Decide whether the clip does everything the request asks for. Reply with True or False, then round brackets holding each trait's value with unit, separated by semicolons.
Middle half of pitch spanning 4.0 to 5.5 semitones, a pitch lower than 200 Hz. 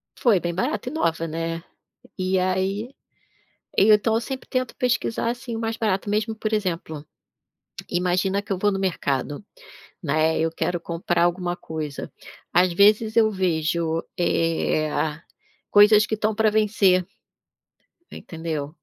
True (4.5 semitones; 185 Hz)